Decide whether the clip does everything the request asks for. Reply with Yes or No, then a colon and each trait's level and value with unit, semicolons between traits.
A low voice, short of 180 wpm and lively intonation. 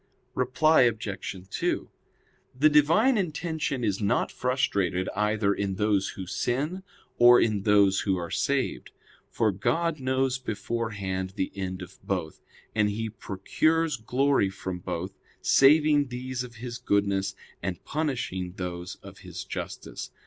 Yes: low, 110 Hz; slow, 135 wpm; wide, 5.7 semitones